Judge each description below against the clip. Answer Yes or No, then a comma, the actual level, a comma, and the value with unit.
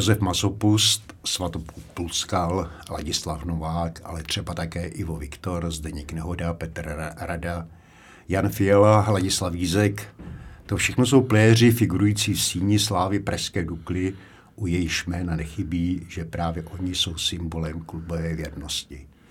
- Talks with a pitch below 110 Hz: Yes, very low, 90 Hz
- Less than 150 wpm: Yes, average, 120 wpm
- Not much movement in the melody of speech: No, average, 3.3 semitones